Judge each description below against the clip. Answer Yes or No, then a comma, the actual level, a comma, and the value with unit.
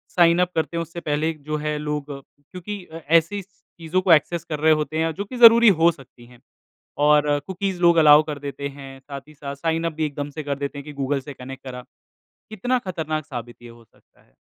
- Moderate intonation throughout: Yes, average, 3.4 semitones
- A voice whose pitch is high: No, medium, 155 Hz